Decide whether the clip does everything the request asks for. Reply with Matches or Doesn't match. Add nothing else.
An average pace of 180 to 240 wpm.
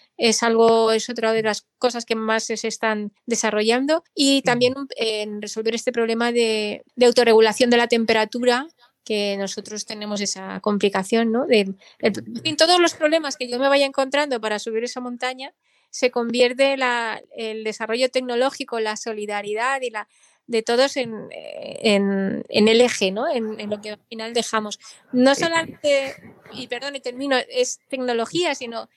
Doesn't match